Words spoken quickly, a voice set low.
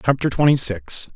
No: average, 155 wpm; low, 125 Hz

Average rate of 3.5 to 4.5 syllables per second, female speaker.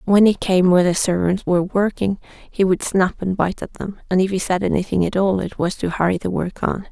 No: 5.6 syllables/s; female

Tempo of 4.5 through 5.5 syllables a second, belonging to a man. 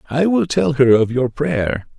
No: 4.1 syllables/s; male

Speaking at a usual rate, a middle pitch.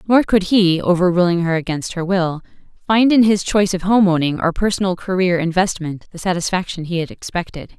Yes: average, 185 wpm; medium, 180 Hz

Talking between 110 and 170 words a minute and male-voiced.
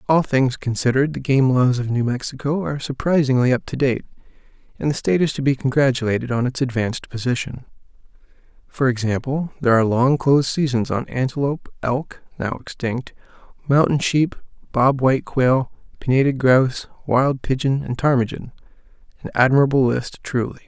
Yes: average, 150 wpm; male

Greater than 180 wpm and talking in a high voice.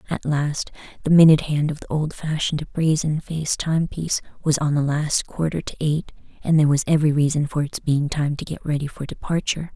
No: average, 195 wpm; medium, 150 Hz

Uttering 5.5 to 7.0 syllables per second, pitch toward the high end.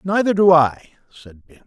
No: 6.4 syllables/s; medium, 165 Hz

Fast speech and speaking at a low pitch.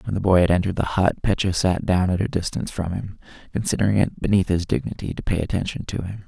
Yes: fast, 240 wpm; very low, 95 Hz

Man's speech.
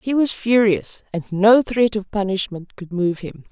No: female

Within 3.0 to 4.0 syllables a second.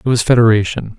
No: 6.3 syllables/s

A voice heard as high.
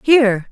Yes: high, 240 Hz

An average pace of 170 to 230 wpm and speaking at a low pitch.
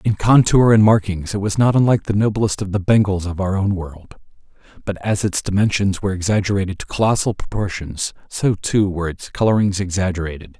Yes: average, 180 wpm; low, 100 Hz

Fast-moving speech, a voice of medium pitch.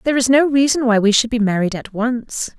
No: fast, 255 wpm; high, 240 Hz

